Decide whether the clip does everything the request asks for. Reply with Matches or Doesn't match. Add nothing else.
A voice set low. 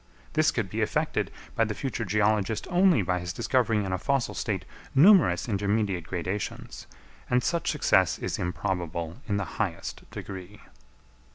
Matches